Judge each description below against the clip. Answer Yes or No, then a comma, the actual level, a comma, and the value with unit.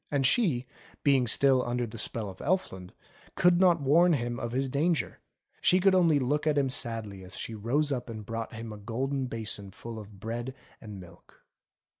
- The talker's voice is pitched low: Yes, low, 125 Hz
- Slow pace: No, average, 190 wpm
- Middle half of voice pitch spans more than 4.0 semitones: Yes, average, 4.5 semitones